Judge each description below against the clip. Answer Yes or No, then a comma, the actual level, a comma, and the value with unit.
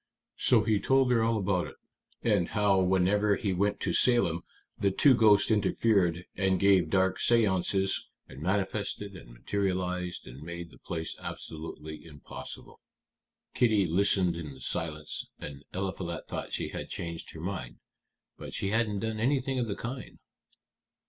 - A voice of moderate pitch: No, very low, 95 Hz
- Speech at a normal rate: Yes, average, 150 wpm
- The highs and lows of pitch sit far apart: No, average, 3.7 semitones